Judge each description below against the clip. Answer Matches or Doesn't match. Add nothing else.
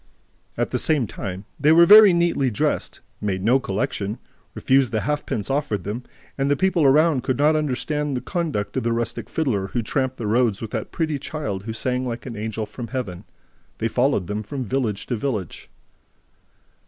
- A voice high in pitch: Doesn't match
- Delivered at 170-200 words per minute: Matches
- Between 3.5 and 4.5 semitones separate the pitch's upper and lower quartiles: Doesn't match